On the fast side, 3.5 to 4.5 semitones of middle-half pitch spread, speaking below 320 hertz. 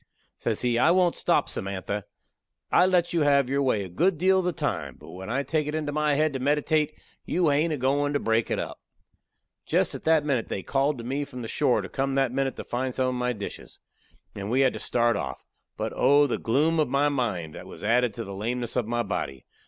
Yes: fast, 240 wpm; average, 4.1 semitones; low, 135 Hz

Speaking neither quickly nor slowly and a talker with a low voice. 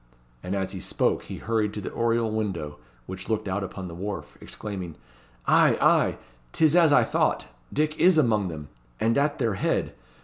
Yes: average, 190 wpm; low, 105 Hz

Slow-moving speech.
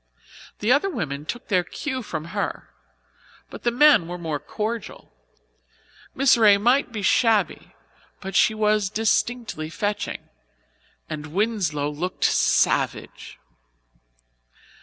Yes: slow, 115 wpm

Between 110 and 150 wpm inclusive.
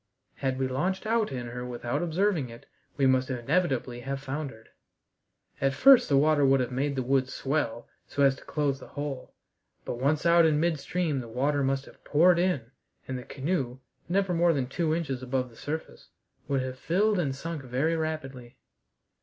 No: average, 185 wpm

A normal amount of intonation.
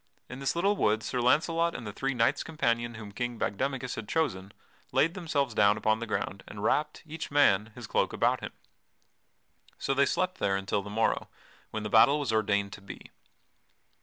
No: wide, 5.7 semitones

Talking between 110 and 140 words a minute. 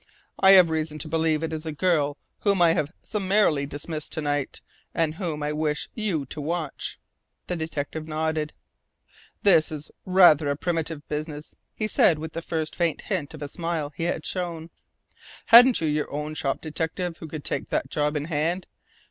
No: average, 180 wpm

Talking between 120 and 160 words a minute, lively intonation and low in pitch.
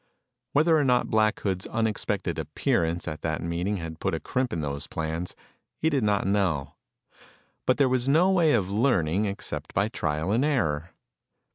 No: average, 170 wpm; wide, 7.5 semitones; low, 100 Hz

